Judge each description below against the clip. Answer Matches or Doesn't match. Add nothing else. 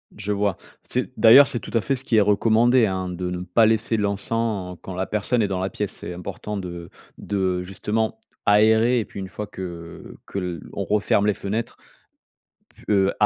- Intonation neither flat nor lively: Matches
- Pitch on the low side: Matches